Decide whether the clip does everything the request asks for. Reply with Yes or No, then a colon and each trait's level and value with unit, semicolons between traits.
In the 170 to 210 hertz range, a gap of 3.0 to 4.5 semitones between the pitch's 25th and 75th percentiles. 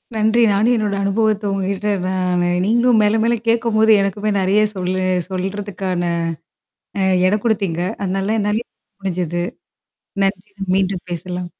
No: high, 200 Hz; narrow, 2.5 semitones